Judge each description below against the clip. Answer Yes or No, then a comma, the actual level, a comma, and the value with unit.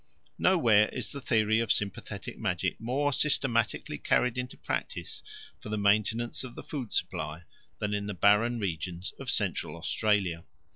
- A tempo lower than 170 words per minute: Yes, average, 150 wpm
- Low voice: Yes, low, 110 Hz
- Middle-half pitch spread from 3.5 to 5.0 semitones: No, average, 3.0 semitones